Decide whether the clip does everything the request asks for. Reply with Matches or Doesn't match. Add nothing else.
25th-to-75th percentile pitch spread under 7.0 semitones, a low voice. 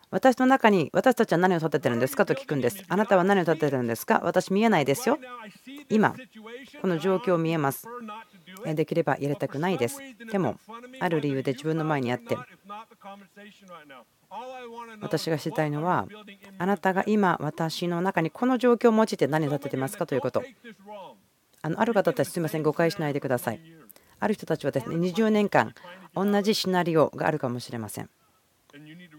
Doesn't match